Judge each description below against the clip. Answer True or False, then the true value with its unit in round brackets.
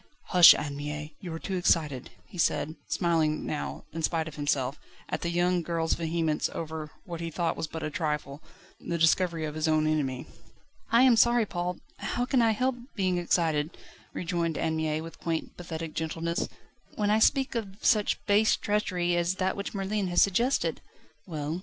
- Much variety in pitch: False (3.4 semitones)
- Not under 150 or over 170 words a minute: False (180 wpm)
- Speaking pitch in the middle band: True (170 Hz)